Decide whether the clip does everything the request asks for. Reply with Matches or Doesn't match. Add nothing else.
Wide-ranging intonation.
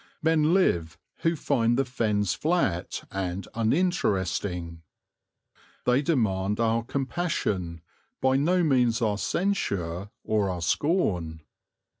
Matches